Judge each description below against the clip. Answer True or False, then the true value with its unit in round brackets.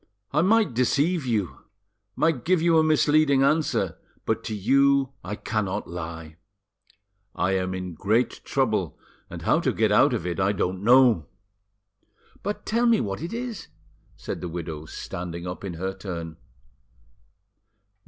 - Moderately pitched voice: False (110 Hz)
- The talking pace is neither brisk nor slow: True (150 wpm)